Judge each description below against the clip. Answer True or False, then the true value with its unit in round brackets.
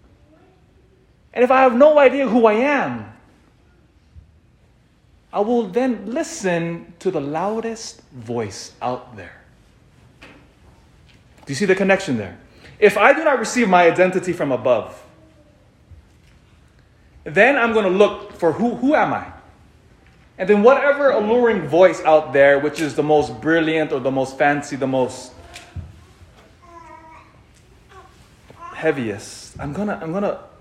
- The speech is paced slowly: True (130 wpm)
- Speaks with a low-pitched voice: False (180 Hz)